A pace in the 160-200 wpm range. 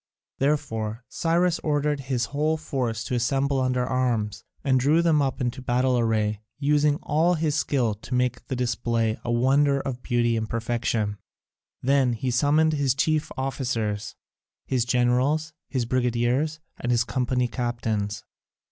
No: average, 145 wpm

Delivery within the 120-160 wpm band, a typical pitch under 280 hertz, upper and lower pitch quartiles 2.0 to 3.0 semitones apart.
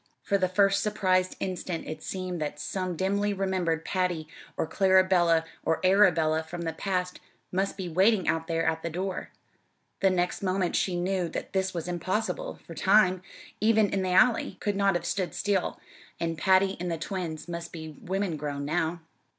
No: average, 175 wpm; medium, 185 Hz; narrow, 2.6 semitones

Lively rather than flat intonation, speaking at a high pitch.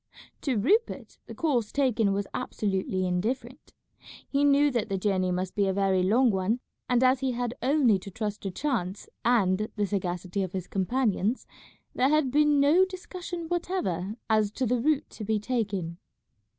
Yes: wide, 5.8 semitones; high, 220 Hz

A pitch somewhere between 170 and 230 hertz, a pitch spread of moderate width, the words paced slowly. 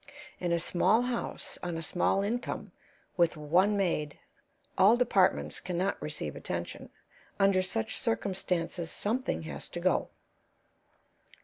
Yes: medium, 185 Hz; average, 3.0 semitones; slow, 125 wpm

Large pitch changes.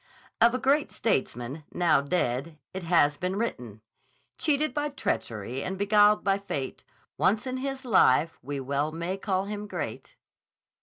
Yes: wide, 7.9 semitones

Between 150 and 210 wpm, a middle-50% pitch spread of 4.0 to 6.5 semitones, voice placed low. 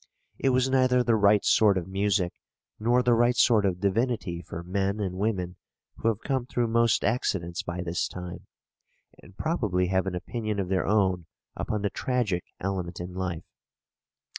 Yes: average, 170 wpm; average, 4.3 semitones; low, 100 Hz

